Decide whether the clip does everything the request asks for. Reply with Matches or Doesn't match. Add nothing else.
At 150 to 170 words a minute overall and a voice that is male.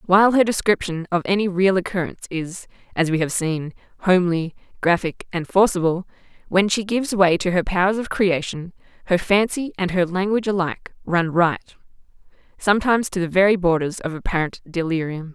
Doesn't match